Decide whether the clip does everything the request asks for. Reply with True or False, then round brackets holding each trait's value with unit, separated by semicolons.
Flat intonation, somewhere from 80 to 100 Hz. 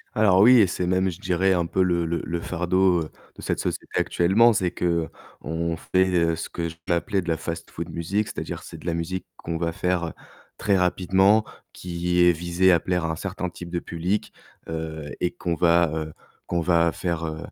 True (1.8 semitones; 85 Hz)